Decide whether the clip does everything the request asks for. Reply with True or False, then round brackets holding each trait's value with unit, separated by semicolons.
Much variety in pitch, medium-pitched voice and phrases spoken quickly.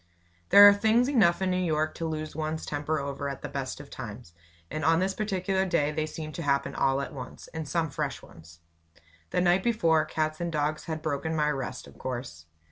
False (3.7 semitones; 155 Hz; 210 wpm)